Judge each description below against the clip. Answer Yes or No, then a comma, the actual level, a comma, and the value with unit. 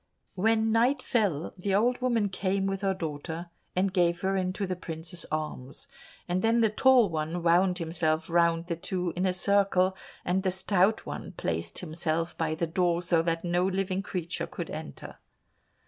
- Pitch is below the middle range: No, medium, 180 Hz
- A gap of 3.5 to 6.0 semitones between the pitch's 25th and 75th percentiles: No, average, 2.7 semitones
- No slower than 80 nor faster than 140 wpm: No, average, 175 wpm